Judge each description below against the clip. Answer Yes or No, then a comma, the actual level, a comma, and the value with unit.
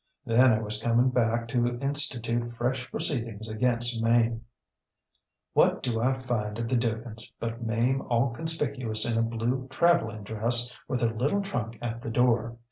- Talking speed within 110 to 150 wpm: No, average, 160 wpm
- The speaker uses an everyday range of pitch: No, narrow, 1.9 semitones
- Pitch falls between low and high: No, low, 120 Hz